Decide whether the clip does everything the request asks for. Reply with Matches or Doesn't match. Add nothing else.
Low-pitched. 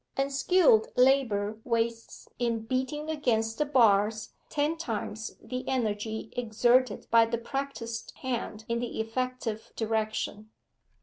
Doesn't match